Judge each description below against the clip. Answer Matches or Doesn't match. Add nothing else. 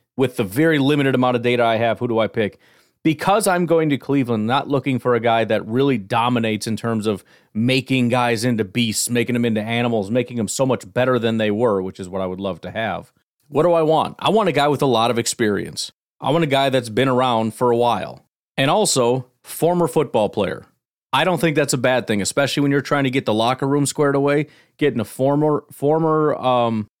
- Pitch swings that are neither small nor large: Matches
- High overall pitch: Doesn't match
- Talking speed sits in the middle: Doesn't match